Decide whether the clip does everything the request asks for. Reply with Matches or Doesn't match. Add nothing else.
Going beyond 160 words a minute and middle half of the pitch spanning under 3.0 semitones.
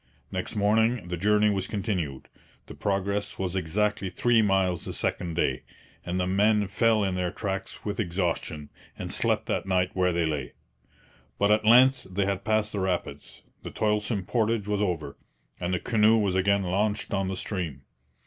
Matches